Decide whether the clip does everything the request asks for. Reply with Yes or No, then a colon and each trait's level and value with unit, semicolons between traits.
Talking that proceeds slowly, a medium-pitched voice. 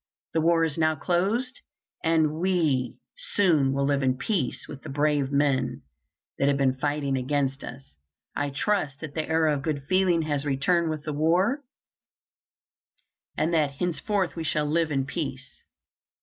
No: average, 160 wpm; medium, 150 Hz